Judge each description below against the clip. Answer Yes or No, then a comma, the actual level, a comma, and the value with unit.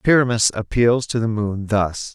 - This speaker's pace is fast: No, average, 170 wpm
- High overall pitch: No, low, 110 Hz